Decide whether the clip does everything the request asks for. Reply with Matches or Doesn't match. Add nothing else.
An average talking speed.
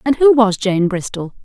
Doesn't match